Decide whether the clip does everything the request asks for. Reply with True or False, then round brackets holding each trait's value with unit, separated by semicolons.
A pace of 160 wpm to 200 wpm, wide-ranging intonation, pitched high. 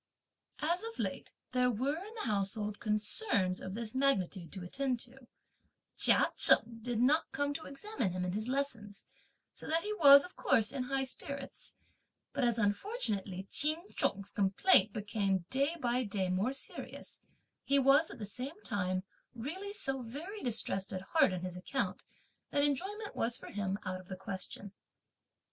True (165 wpm; 6.2 semitones; 245 Hz)